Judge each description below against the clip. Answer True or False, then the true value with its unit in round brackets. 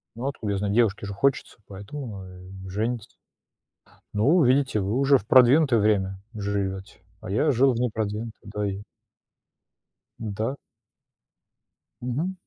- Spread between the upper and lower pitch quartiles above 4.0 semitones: True (4.4 semitones)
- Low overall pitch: True (110 Hz)